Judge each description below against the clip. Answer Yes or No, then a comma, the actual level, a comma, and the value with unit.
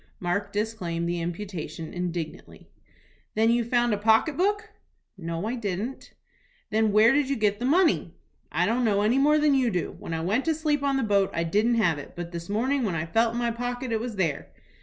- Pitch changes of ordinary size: No, wide, 5.9 semitones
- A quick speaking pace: Yes, fast, 215 wpm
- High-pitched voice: Yes, high, 220 Hz